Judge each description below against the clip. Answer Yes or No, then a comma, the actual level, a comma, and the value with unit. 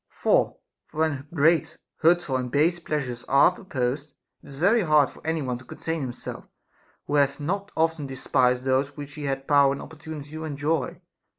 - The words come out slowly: No, average, 175 wpm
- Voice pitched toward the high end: No, medium, 145 Hz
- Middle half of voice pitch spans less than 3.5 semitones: Yes, average, 2.9 semitones